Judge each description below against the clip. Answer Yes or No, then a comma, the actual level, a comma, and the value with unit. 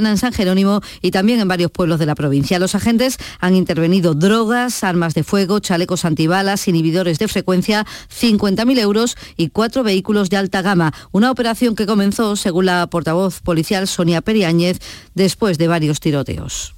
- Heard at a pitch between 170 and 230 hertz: Yes, high, 190 Hz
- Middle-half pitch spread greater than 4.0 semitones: No, average, 3.7 semitones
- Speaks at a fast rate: No, average, 165 wpm